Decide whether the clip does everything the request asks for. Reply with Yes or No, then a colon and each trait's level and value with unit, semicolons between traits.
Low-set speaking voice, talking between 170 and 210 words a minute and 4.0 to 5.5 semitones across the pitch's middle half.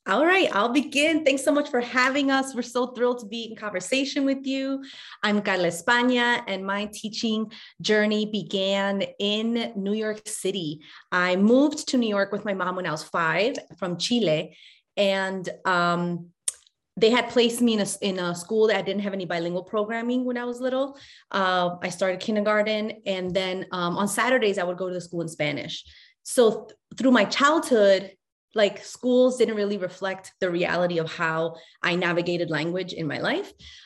No: high, 205 Hz; average, 185 wpm; average, 4.7 semitones